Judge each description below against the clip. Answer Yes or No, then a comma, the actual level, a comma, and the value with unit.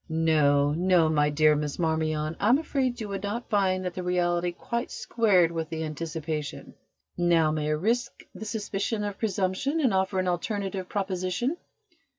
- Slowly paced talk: No, average, 165 wpm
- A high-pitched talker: No, medium, 180 Hz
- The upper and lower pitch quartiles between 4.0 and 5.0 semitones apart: Yes, average, 4.4 semitones